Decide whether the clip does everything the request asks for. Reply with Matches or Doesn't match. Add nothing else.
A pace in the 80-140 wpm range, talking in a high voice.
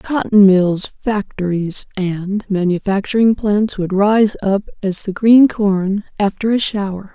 Matches